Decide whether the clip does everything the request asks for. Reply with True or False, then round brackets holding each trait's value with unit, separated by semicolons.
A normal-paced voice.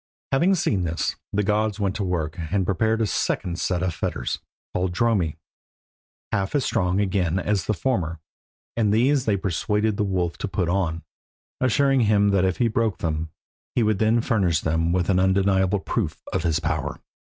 True (180 wpm)